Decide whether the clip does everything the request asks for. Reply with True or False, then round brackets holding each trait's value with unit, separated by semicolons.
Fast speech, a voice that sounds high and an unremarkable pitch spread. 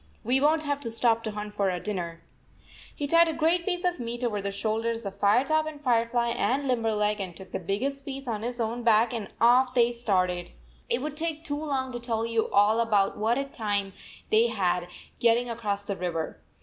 True (220 wpm; 230 Hz; 4.3 semitones)